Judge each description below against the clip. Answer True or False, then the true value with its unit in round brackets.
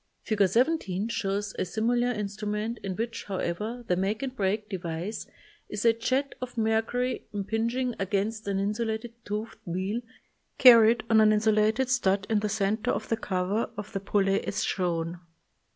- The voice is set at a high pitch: True (215 Hz)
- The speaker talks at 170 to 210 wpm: False (160 wpm)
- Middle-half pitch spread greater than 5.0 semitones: False (2.7 semitones)